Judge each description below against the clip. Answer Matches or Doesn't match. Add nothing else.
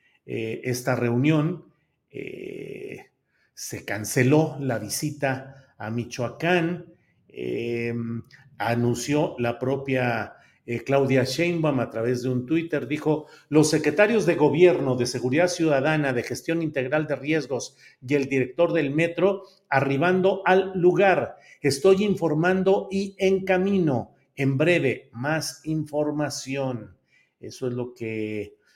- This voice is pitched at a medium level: Matches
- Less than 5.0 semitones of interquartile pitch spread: Doesn't match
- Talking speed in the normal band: Doesn't match